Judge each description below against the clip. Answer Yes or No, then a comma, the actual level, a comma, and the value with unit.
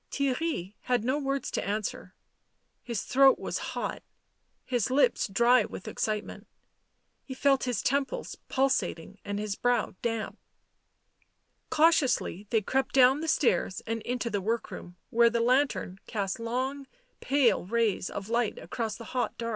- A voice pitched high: Yes, high, 235 Hz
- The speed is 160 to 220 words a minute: No, average, 150 wpm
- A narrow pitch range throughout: No, average, 3.9 semitones